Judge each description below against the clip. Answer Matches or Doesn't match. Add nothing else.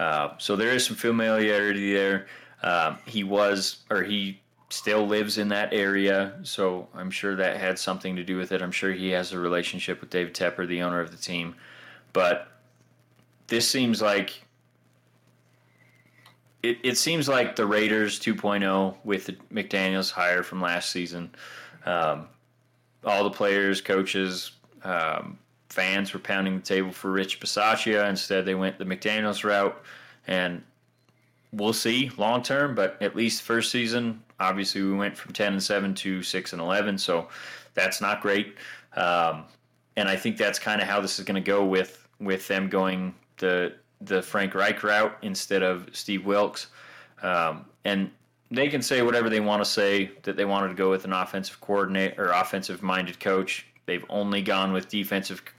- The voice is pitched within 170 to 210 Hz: Doesn't match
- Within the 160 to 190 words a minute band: Matches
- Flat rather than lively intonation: Matches